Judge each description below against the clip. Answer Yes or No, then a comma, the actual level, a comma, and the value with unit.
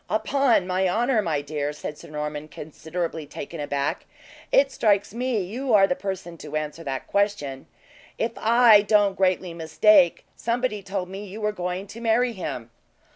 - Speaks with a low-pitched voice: No, high, 190 Hz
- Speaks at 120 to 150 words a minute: No, average, 165 wpm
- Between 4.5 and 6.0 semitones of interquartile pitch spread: Yes, wide, 5.6 semitones